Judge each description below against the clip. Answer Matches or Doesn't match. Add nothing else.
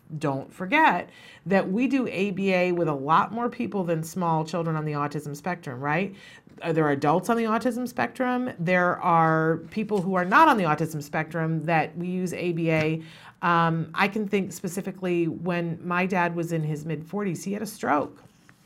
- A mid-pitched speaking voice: Matches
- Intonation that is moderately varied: Matches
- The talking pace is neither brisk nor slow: Matches